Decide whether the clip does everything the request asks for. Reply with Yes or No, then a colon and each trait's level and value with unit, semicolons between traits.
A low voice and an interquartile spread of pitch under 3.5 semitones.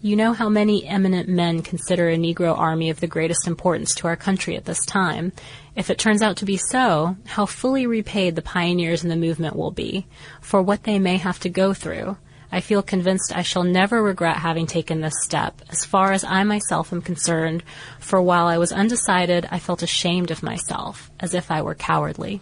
No: medium, 180 Hz; average, 2.8 semitones